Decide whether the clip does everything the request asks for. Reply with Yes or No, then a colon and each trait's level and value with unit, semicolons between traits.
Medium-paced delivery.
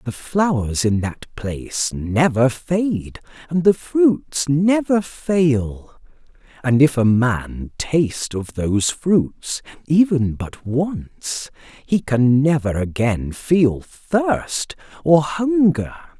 No: slow, 115 wpm